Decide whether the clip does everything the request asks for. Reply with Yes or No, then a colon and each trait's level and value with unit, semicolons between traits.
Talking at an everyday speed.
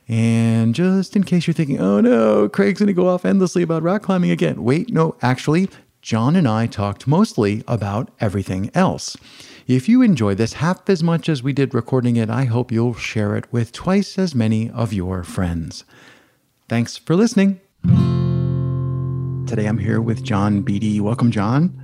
Yes: average, 175 wpm